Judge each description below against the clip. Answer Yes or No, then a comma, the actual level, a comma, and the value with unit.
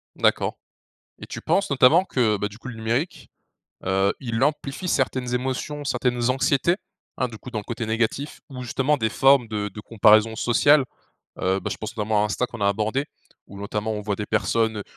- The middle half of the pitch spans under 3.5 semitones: No, average, 3.8 semitones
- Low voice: Yes, low, 115 Hz